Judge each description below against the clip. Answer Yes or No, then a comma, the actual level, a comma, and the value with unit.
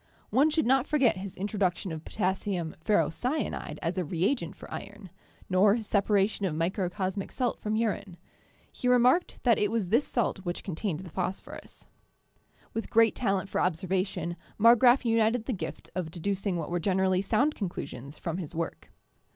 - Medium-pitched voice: No, high, 195 Hz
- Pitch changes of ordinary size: Yes, average, 4.3 semitones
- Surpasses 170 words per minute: No, average, 160 wpm